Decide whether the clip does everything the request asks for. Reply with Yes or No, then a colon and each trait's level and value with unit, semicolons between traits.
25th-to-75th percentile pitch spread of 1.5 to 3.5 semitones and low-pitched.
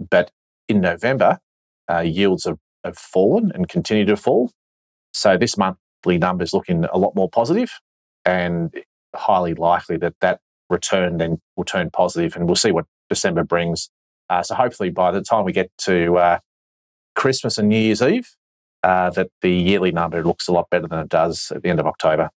Yes: average, 3.0 semitones; very low, 85 Hz